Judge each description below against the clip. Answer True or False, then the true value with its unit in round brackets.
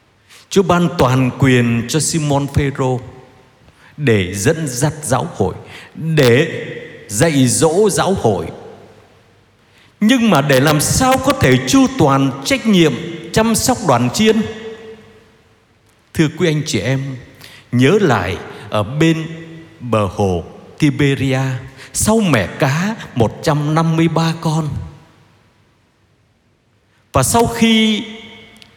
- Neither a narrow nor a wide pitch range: False (5.9 semitones)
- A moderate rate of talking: False (110 wpm)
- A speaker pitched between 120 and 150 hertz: True (140 Hz)